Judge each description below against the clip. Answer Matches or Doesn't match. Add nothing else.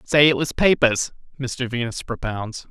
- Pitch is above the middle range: Doesn't match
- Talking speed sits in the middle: Matches